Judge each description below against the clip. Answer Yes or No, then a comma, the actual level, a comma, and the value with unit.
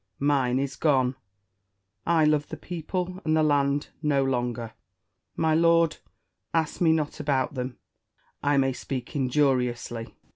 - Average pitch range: Yes, average, 3.4 semitones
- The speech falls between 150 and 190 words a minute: No, slow, 135 wpm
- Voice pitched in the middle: Yes, medium, 145 Hz